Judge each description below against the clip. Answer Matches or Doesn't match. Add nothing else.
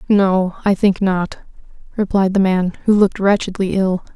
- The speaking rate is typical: Matches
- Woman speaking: Matches